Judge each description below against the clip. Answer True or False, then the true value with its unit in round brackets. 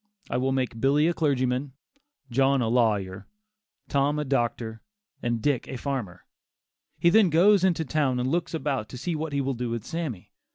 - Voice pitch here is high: False (135 Hz)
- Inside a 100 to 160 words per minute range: False (180 wpm)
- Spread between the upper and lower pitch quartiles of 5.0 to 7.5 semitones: False (4.2 semitones)